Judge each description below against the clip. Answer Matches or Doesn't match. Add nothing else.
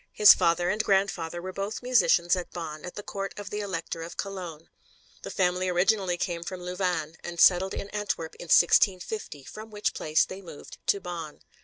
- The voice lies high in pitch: Doesn't match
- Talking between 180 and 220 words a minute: Matches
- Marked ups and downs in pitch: Doesn't match